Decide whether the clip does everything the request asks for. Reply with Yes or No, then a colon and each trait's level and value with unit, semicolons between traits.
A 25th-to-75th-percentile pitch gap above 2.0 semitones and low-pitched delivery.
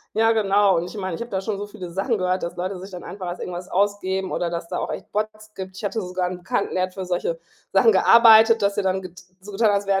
No: narrow, 2.4 semitones; high, 195 Hz